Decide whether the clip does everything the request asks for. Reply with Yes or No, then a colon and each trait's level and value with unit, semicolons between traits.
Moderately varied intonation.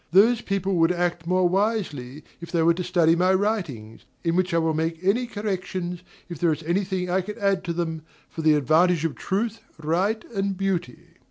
Yes: average, 3.0 semitones